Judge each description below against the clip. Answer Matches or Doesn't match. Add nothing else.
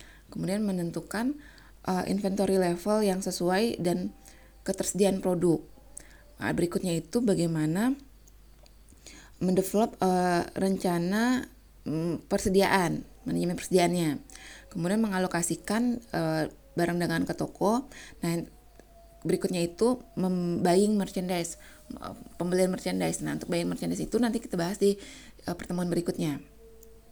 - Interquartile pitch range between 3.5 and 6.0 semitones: Doesn't match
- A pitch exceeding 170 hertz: Matches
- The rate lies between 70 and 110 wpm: Matches